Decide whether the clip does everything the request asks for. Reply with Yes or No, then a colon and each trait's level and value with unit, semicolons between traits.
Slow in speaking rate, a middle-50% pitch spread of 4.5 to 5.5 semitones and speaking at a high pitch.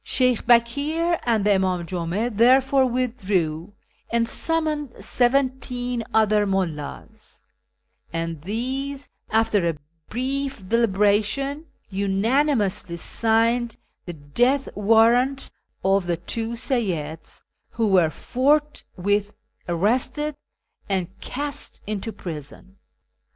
Yes: slow, 100 wpm; average, 5.2 semitones; high, 225 Hz